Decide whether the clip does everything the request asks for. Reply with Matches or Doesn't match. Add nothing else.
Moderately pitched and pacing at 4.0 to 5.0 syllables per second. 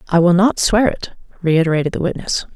Doesn't match